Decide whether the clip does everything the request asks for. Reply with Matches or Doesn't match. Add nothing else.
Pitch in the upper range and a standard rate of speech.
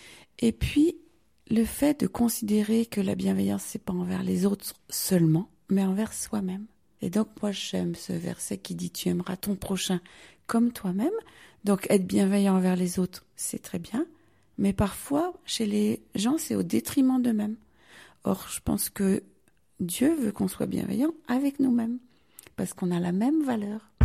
Matches